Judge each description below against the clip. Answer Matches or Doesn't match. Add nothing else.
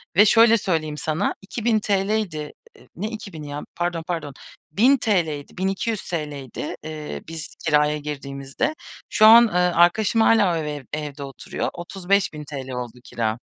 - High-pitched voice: Doesn't match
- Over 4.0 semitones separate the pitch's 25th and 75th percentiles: Matches